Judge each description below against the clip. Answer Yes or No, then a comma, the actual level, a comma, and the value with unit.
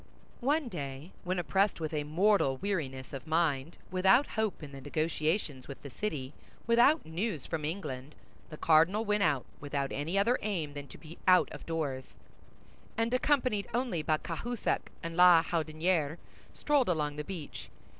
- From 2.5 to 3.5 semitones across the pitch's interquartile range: No, wide, 5.5 semitones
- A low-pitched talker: No, medium, 165 Hz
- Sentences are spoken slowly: No, average, 160 wpm